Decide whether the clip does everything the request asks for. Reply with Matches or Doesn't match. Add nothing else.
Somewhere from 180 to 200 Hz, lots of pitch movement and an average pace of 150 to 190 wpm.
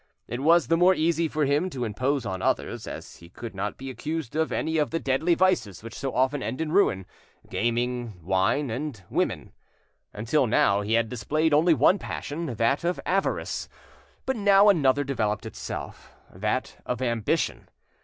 Doesn't match